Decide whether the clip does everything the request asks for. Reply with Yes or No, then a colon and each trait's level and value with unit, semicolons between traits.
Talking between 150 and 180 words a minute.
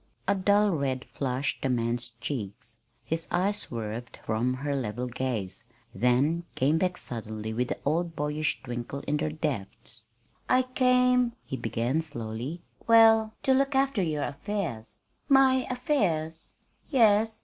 No: average, 140 wpm